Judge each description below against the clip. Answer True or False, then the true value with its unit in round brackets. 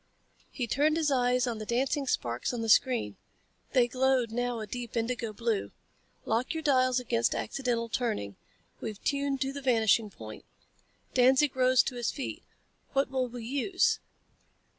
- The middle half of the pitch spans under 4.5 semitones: True (2.6 semitones)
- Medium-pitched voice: False (250 Hz)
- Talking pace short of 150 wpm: False (160 wpm)